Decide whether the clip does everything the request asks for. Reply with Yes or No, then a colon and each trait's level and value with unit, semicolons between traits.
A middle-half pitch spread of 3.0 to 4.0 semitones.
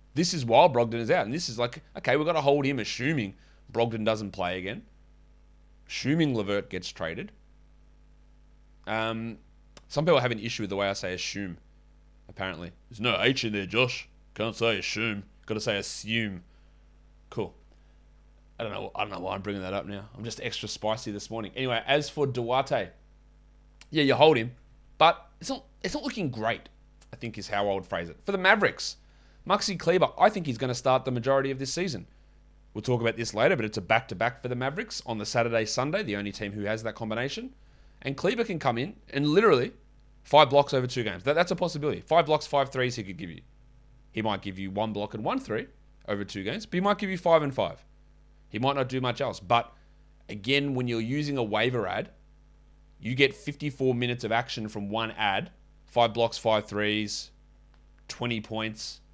No: average, 4.7 semitones